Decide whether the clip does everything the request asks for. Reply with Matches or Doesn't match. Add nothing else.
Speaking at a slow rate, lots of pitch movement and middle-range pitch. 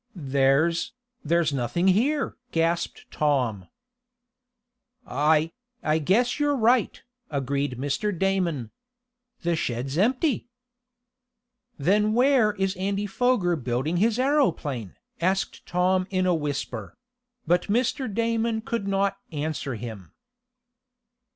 Matches